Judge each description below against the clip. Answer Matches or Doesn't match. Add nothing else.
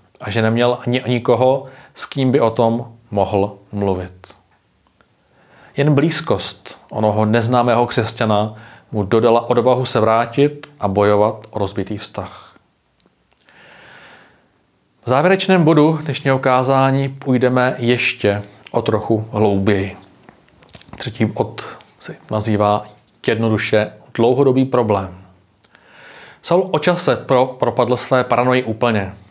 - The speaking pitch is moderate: Doesn't match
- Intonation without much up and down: Doesn't match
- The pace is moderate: Doesn't match